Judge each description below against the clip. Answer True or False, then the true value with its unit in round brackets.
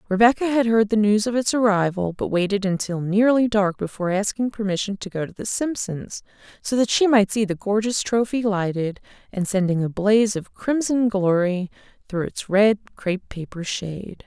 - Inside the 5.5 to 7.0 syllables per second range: False (5.1 syllables/s)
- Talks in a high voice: True (205 Hz)